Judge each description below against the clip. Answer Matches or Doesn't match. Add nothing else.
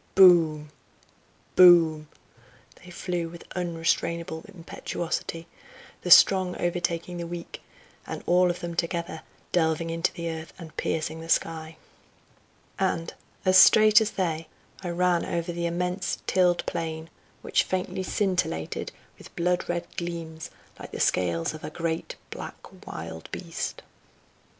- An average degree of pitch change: Doesn't match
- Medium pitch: Matches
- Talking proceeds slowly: Matches